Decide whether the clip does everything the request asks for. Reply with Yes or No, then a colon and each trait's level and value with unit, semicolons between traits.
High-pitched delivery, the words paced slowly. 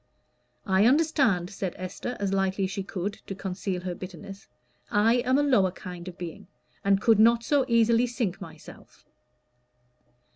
No: high, 200 Hz; average, 155 wpm